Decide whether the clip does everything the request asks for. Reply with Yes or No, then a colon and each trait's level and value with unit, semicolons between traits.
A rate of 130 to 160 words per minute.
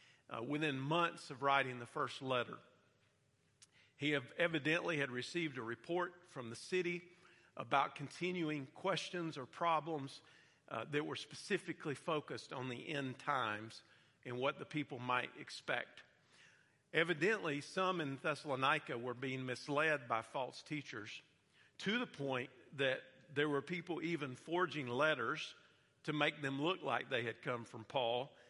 Yes: average, 140 wpm